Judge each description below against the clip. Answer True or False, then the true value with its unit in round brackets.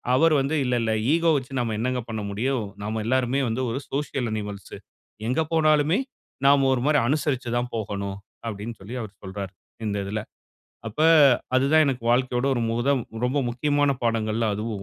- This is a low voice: True (120 Hz)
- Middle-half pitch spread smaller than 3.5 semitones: False (3.9 semitones)